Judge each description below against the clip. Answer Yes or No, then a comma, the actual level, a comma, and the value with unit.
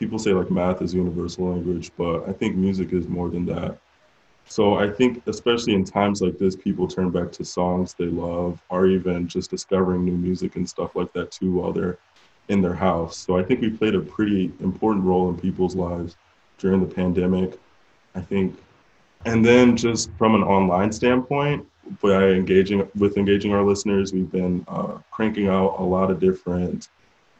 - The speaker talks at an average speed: Yes, average, 185 wpm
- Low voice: Yes, very low, 95 Hz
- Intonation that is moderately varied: No, narrow, 2.0 semitones